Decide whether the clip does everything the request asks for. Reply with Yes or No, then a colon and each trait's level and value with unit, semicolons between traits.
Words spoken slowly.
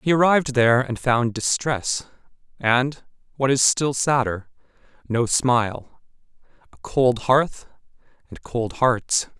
Yes: slow, 120 wpm